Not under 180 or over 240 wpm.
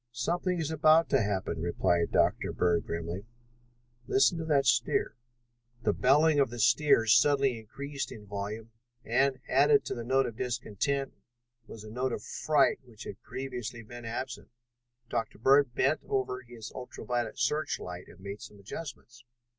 No: average, 160 wpm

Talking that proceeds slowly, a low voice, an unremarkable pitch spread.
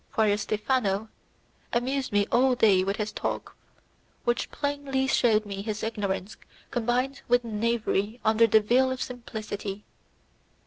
No: slow, 130 wpm; high, 225 Hz; average, 3.2 semitones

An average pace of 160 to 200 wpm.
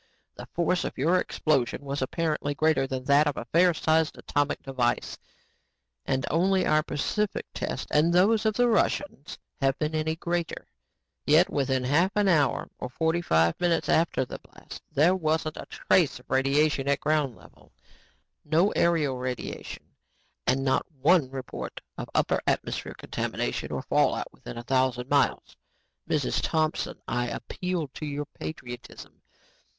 No: average, 150 wpm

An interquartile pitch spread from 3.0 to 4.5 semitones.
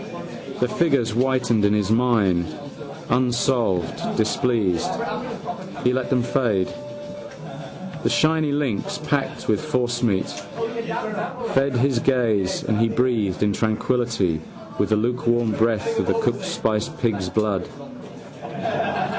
Yes: average, 3.4 semitones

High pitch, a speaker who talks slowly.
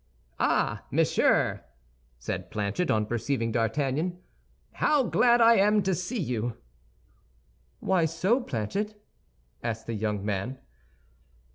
No: medium, 140 Hz; slow, 110 wpm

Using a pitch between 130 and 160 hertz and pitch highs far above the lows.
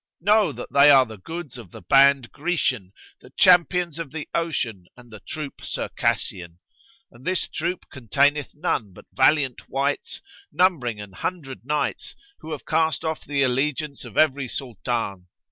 No: medium, 140 Hz; average, 4.9 semitones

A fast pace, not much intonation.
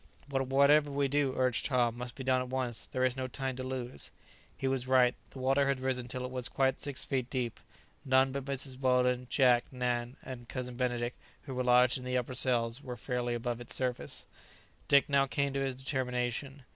Yes: fast, 210 wpm; narrow, 1.3 semitones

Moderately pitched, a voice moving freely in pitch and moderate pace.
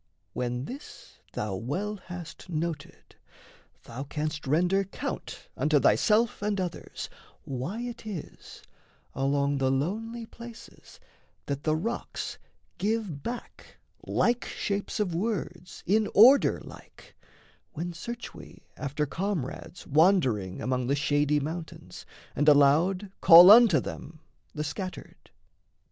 No: medium, 170 Hz; wide, 6.4 semitones; slow, 115 wpm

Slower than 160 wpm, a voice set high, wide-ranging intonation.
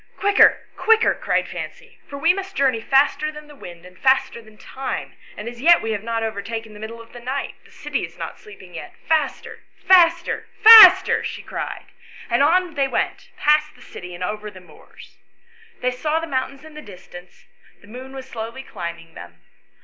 No: average, 195 wpm; very high, 260 Hz; wide, 6.4 semitones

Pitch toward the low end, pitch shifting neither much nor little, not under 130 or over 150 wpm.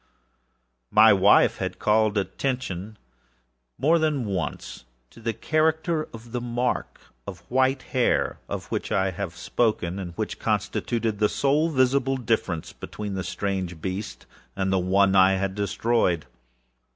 Yes: low, 105 Hz; average, 4.9 semitones; average, 140 wpm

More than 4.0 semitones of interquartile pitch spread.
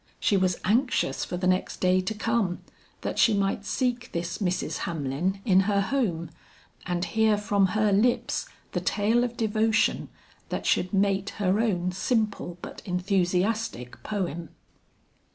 No: average, 3.3 semitones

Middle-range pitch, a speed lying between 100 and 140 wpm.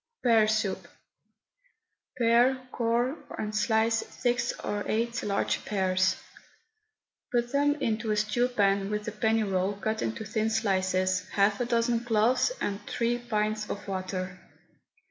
No: high, 215 Hz; slow, 135 wpm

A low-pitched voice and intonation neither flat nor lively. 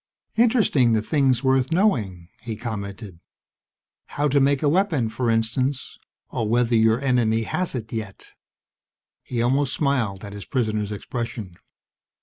Yes: low, 120 Hz; average, 3.9 semitones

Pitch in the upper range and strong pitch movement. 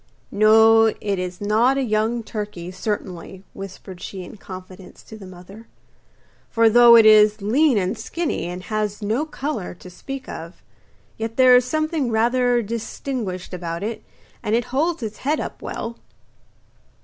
No: high, 215 Hz; average, 4.1 semitones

